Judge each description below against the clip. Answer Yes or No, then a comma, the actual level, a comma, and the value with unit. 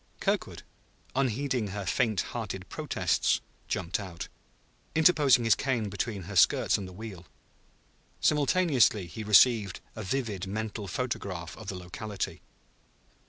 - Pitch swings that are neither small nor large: Yes, average, 4.9 semitones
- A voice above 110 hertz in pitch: No, low, 105 Hz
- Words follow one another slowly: Yes, slow, 120 wpm